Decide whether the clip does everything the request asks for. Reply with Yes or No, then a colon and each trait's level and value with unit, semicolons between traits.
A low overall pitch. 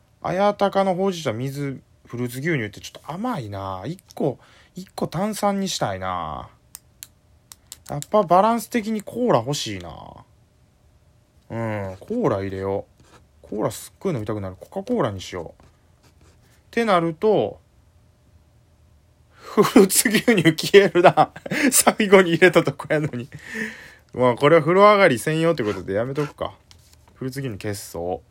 No: medium, 145 Hz